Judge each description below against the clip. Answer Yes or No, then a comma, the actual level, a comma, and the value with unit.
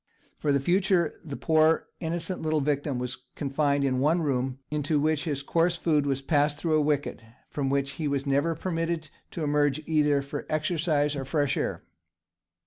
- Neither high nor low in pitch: Yes, medium, 150 Hz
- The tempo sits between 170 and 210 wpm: Yes, average, 180 wpm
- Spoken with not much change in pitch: Yes, narrow, 2.3 semitones